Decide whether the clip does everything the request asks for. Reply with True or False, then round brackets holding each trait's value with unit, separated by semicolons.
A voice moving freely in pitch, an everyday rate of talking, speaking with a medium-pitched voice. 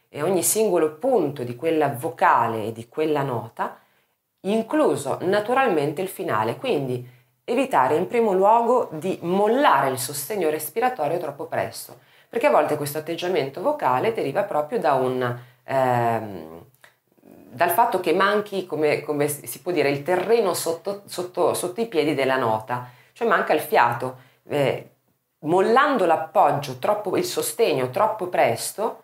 True (7.5 semitones; 140 wpm; 155 Hz)